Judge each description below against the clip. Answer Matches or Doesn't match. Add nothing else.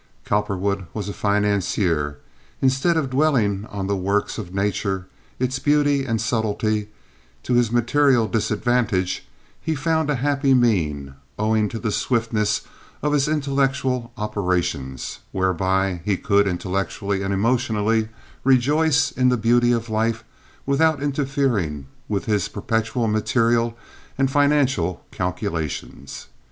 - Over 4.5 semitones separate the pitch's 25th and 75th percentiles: Matches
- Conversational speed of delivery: Doesn't match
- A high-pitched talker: Doesn't match